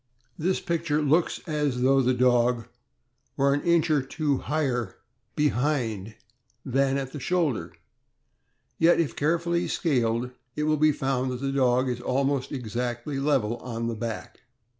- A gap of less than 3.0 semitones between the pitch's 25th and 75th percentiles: No, average, 3.6 semitones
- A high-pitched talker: No, low, 135 Hz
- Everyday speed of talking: Yes, average, 145 wpm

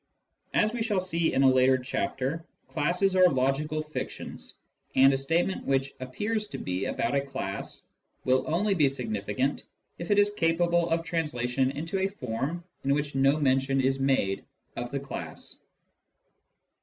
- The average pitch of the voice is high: No, medium, 140 Hz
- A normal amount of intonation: Yes, average, 4.6 semitones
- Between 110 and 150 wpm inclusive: No, average, 160 wpm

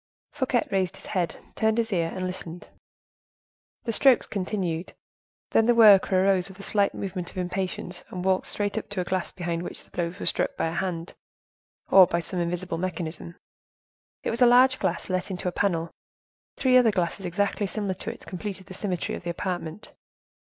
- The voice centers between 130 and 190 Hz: Yes, medium, 185 Hz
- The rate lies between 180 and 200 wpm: Yes, average, 190 wpm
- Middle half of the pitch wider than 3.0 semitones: No, narrow, 2.6 semitones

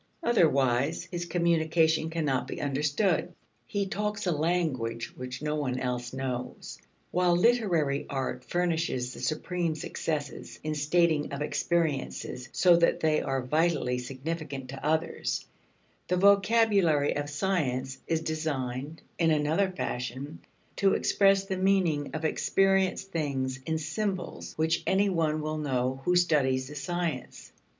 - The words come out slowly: Yes, slow, 130 wpm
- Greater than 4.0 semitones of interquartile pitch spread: Yes, average, 4.5 semitones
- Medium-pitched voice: Yes, medium, 155 Hz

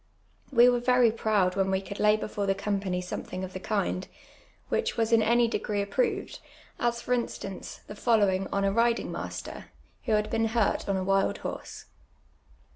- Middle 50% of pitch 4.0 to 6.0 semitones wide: No, average, 3.1 semitones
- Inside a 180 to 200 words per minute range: Yes, average, 190 wpm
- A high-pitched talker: Yes, high, 210 Hz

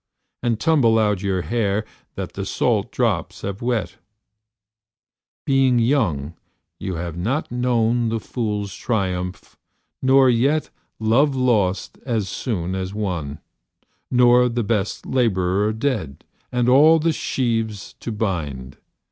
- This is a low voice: Yes, low, 110 Hz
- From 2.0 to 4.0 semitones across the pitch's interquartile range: No, average, 4.7 semitones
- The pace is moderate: No, slow, 120 wpm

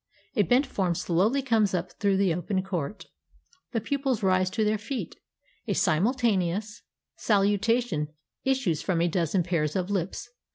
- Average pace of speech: Yes, average, 150 wpm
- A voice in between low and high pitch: No, high, 195 Hz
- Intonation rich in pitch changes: No, average, 4.2 semitones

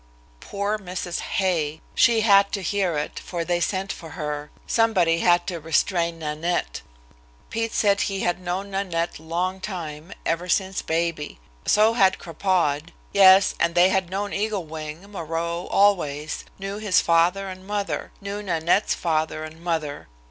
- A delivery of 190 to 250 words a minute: No, average, 150 wpm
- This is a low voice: No, medium, 175 Hz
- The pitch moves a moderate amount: Yes, average, 3.2 semitones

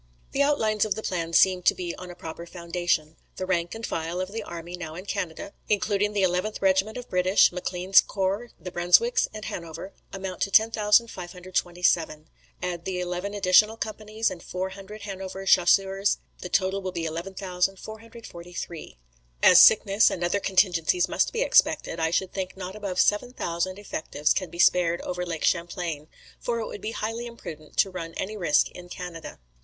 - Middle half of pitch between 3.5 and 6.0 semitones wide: No, average, 2.9 semitones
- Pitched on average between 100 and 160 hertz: No, medium, 185 Hz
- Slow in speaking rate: No, average, 170 wpm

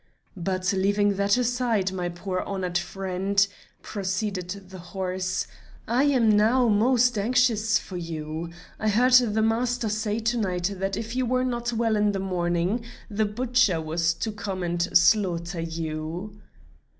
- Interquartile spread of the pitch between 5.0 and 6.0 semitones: No, average, 3.8 semitones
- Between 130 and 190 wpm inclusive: Yes, average, 150 wpm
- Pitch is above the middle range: Yes, high, 200 Hz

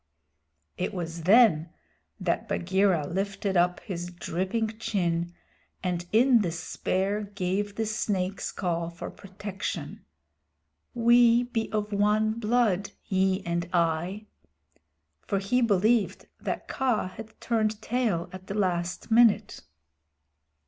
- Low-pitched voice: No, high, 195 Hz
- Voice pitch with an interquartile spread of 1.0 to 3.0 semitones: No, average, 3.6 semitones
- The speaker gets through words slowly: Yes, slow, 115 wpm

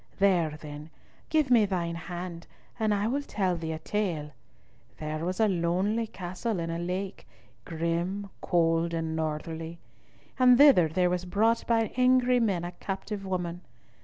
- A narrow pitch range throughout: No, average, 4.0 semitones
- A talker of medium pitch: Yes, medium, 180 Hz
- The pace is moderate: Yes, average, 155 wpm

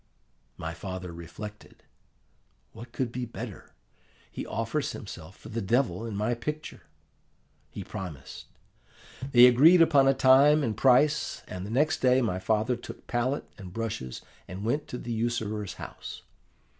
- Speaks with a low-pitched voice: Yes, low, 115 Hz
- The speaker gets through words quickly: No, average, 145 wpm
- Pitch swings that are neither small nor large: Yes, average, 4.9 semitones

